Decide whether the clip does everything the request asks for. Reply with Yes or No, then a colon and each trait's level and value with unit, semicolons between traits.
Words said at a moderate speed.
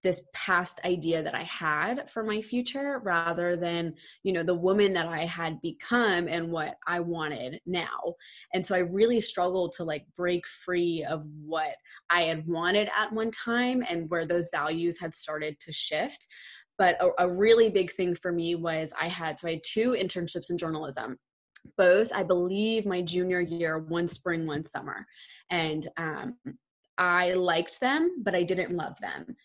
Yes: average, 175 wpm